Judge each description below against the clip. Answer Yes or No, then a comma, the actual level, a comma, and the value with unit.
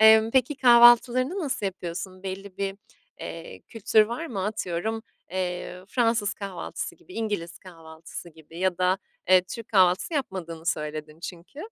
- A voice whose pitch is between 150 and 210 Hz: Yes, high, 190 Hz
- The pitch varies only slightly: No, average, 4.7 semitones